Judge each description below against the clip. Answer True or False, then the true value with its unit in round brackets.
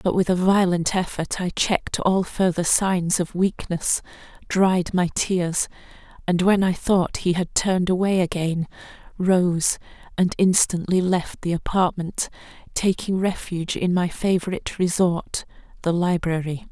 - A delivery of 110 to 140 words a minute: True (135 wpm)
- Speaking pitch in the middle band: True (180 Hz)